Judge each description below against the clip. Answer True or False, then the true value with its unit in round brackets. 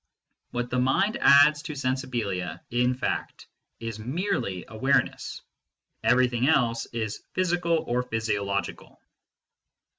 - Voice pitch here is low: True (125 Hz)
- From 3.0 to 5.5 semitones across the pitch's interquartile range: True (3.8 semitones)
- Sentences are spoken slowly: True (110 wpm)